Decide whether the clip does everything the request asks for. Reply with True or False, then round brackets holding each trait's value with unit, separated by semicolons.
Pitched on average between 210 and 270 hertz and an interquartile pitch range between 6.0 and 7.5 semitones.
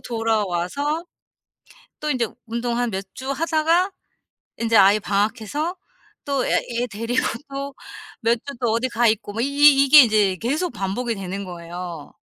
False (235 Hz; 5.3 semitones)